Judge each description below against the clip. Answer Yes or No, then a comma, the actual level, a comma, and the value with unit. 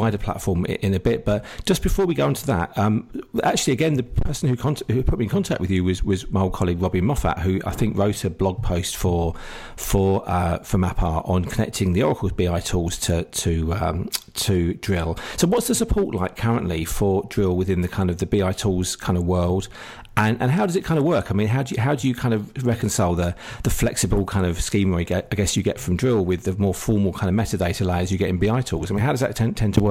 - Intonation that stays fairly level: No, average, 4.1 semitones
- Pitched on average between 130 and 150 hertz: No, low, 100 Hz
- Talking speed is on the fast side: Yes, fast, 255 wpm